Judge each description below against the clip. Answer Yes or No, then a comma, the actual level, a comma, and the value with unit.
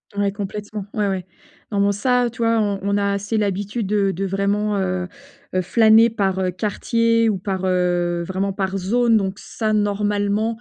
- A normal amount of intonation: No, narrow, 2.0 semitones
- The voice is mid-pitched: No, high, 200 Hz